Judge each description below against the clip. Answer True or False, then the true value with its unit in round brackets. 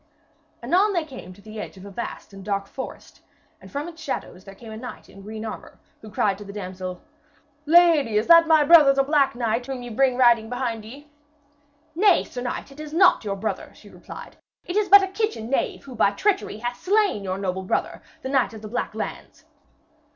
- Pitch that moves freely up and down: True (6.9 semitones)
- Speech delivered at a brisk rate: True (210 wpm)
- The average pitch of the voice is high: True (245 Hz)